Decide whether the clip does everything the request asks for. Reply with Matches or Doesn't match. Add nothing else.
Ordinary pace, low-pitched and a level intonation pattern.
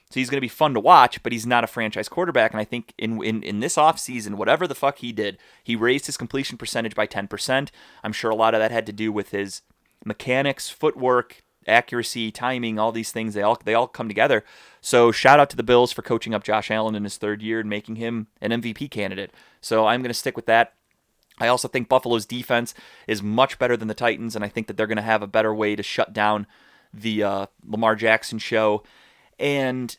Doesn't match